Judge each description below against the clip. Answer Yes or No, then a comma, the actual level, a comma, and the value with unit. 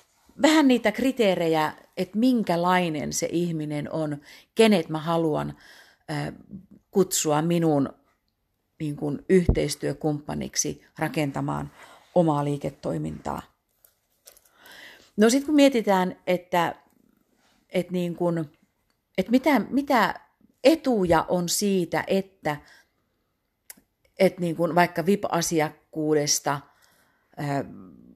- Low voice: No, medium, 170 Hz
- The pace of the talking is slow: Yes, slow, 80 wpm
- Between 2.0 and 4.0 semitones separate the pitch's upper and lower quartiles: No, average, 4.5 semitones